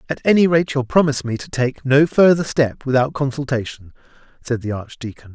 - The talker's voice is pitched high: No, low, 135 Hz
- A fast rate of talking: No, average, 180 wpm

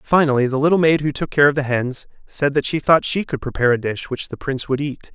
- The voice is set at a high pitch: No, medium, 140 Hz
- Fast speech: Yes, fast, 280 wpm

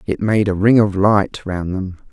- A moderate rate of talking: No, fast, 225 wpm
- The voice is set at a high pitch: No, low, 100 Hz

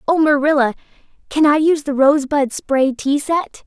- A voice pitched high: Yes, very high, 290 Hz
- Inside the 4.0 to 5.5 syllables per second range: Yes, 5.1 syllables/s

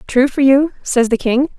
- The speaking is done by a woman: Yes, female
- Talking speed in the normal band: No, fast, 225 wpm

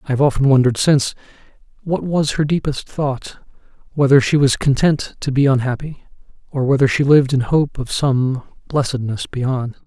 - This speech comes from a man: Yes, male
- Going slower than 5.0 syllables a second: No, 5.2 syllables/s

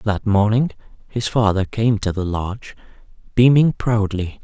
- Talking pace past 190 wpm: No, slow, 135 wpm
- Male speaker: Yes, male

